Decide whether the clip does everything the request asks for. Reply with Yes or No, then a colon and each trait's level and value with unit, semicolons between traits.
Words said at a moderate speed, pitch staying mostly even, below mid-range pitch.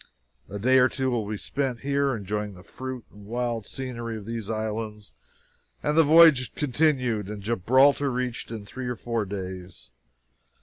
No: average, 165 wpm; average, 3.8 semitones; low, 115 Hz